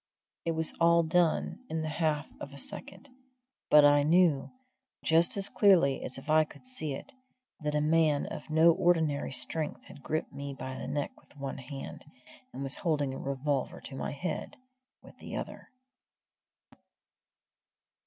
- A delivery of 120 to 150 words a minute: No, average, 165 wpm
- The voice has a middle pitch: Yes, medium, 150 Hz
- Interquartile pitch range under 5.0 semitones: Yes, average, 2.8 semitones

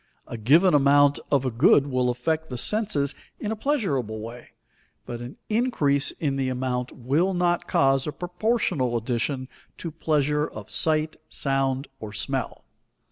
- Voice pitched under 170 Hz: Yes, medium, 140 Hz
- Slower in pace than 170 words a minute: Yes, average, 150 wpm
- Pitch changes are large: No, average, 4.2 semitones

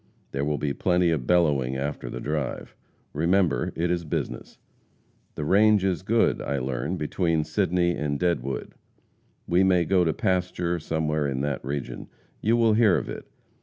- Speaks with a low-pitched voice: Yes, very low, 80 Hz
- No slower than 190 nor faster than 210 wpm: No, average, 165 wpm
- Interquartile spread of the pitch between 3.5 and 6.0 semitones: Yes, average, 4.0 semitones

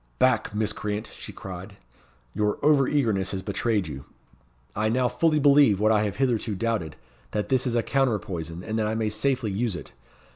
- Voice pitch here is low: Yes, low, 110 Hz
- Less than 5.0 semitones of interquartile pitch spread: Yes, average, 3.8 semitones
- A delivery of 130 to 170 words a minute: No, average, 185 wpm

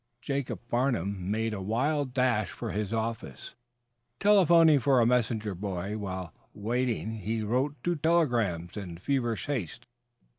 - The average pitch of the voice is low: Yes, low, 115 Hz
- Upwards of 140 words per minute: No, slow, 135 wpm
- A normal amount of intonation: Yes, average, 4.7 semitones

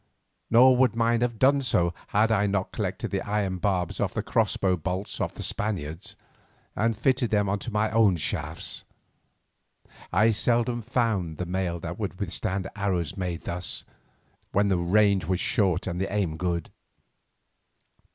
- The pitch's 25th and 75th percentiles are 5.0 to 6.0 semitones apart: No, average, 3.8 semitones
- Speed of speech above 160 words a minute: No, average, 155 wpm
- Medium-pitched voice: No, low, 100 Hz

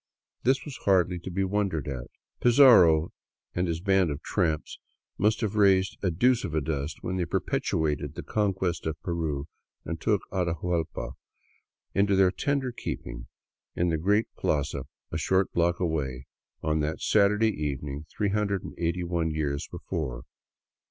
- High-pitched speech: No, very low, 85 Hz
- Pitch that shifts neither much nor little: Yes, average, 4.3 semitones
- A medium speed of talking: Yes, average, 145 wpm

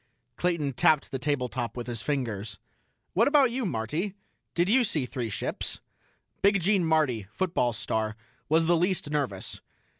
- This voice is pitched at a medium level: Yes, medium, 150 Hz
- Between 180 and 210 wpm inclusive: No, average, 150 wpm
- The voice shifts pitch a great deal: Yes, wide, 7.0 semitones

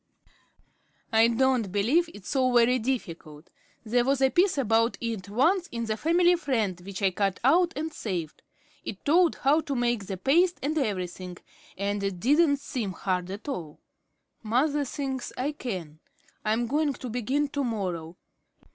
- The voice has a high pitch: Yes, high, 240 Hz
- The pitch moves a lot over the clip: Yes, wide, 6.2 semitones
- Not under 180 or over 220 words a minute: No, average, 160 wpm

